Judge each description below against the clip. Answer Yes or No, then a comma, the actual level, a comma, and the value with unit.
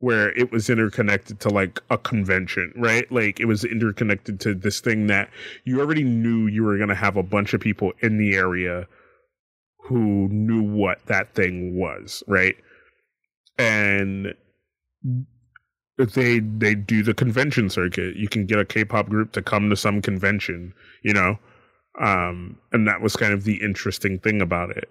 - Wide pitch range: No, narrow, 2.6 semitones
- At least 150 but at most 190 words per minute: Yes, average, 170 wpm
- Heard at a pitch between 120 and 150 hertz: No, low, 105 Hz